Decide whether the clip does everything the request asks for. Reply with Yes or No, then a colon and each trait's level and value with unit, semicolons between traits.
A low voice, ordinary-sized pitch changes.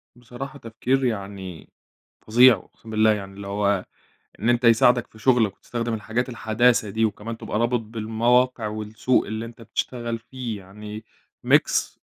No: low, 115 Hz; narrow, 2.3 semitones